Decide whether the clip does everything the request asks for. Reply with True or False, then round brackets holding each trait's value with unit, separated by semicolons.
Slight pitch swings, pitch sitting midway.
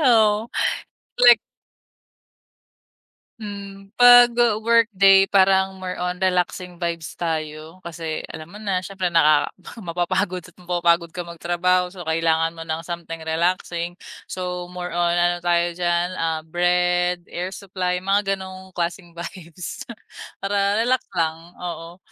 True (2.2 semitones; 180 Hz)